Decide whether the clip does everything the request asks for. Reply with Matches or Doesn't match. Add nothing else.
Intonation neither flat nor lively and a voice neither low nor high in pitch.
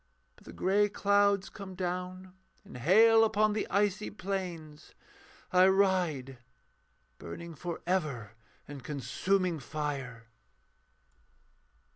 Matches